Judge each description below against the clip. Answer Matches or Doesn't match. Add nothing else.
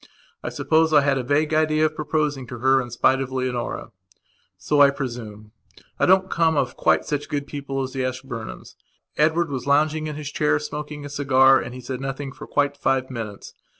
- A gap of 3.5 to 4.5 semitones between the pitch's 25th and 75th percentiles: Doesn't match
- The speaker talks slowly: Doesn't match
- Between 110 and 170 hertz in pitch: Matches